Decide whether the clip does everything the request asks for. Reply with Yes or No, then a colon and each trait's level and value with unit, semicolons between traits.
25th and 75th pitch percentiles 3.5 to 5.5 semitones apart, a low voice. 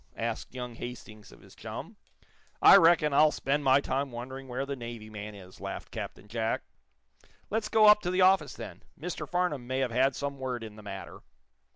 Yes: average, 4.5 semitones; low, 130 Hz